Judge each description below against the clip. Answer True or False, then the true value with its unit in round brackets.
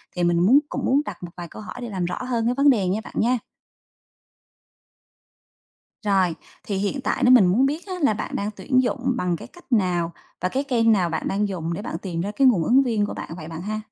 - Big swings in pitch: True (5.7 semitones)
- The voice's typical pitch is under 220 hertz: True (210 Hz)